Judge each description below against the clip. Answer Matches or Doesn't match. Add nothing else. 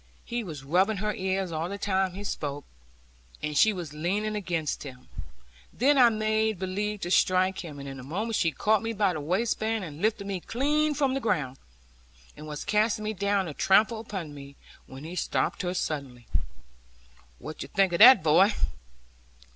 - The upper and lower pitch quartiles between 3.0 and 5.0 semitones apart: Doesn't match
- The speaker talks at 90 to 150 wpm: Doesn't match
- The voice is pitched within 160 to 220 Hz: Matches